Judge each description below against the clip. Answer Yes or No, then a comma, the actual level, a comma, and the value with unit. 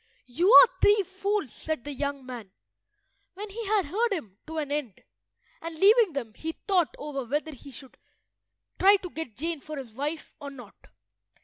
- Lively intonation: Yes, wide, 6.0 semitones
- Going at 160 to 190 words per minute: Yes, average, 180 wpm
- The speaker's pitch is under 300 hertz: No, very high, 310 Hz